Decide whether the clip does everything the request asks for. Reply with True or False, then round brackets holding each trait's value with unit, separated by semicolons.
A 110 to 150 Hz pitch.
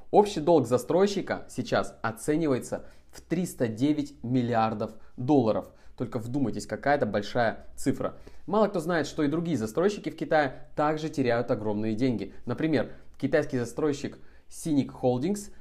True (135 Hz)